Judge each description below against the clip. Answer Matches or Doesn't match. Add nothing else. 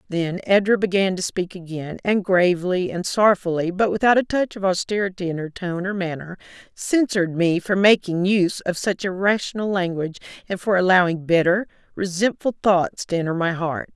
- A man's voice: Doesn't match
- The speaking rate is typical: Matches